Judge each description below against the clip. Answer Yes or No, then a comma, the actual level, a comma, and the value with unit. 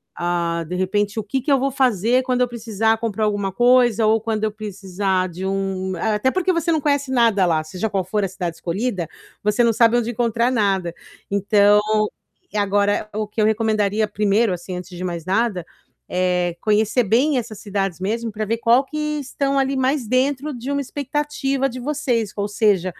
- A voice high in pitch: Yes, high, 215 Hz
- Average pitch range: Yes, average, 4.2 semitones